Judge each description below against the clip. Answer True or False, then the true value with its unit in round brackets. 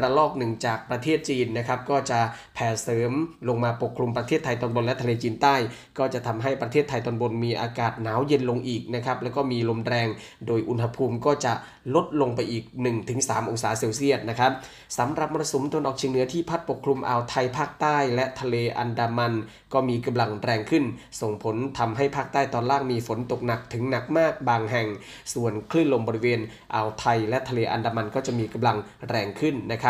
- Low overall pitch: True (120 Hz)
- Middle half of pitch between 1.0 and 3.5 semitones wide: True (2.5 semitones)